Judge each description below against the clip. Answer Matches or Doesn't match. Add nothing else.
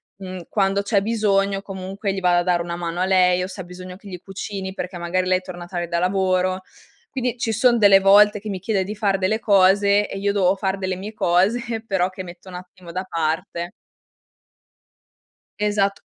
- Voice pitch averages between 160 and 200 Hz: Matches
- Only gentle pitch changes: Matches